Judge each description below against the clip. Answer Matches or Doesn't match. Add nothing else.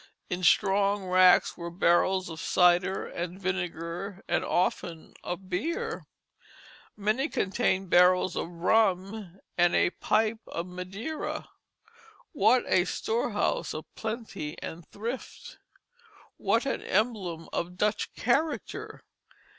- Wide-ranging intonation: Doesn't match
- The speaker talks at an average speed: Doesn't match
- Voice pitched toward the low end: Doesn't match